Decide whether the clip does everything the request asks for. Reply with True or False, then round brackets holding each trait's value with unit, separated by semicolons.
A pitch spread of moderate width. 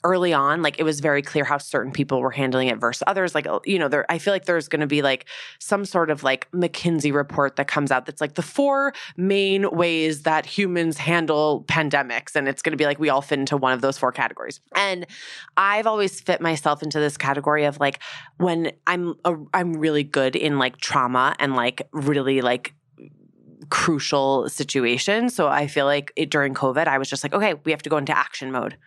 True (3.5 semitones)